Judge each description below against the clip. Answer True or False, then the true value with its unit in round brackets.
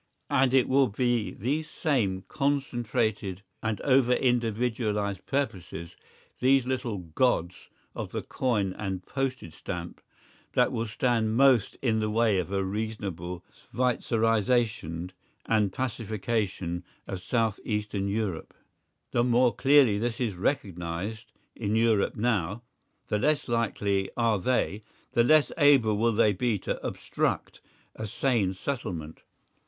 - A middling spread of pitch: True (3.9 semitones)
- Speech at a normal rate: False (125 wpm)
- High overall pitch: False (110 Hz)